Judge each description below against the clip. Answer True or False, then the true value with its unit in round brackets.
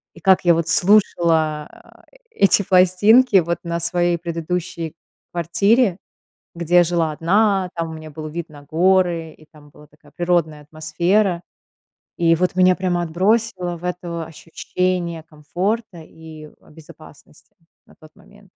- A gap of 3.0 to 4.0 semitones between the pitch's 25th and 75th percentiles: False (2.4 semitones)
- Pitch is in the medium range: True (170 Hz)